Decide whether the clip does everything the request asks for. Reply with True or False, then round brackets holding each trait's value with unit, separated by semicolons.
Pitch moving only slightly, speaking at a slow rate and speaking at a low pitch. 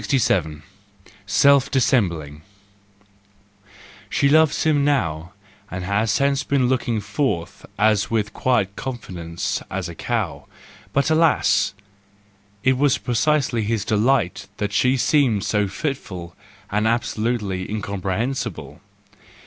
False (5.4 semitones; 110 wpm; 115 Hz)